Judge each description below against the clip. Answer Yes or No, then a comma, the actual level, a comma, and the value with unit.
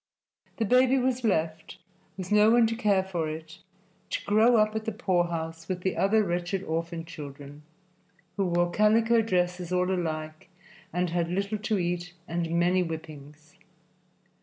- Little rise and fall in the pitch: No, average, 4.3 semitones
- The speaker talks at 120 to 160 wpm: Yes, average, 155 wpm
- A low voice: No, medium, 180 Hz